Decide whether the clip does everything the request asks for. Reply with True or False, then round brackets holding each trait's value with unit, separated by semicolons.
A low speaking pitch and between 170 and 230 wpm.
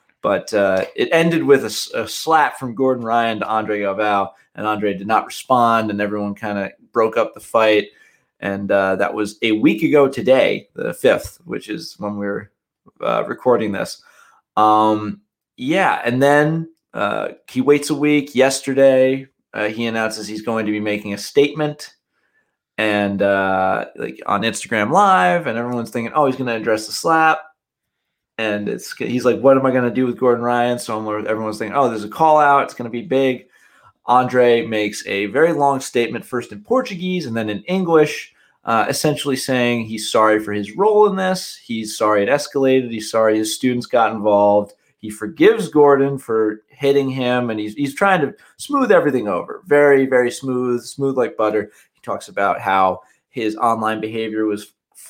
True (120 Hz; 180 wpm)